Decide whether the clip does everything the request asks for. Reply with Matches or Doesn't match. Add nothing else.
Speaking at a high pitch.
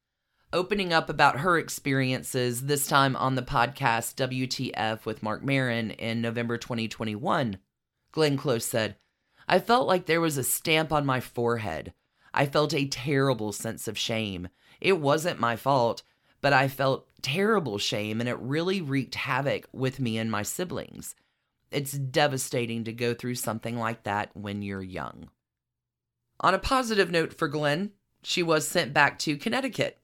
Doesn't match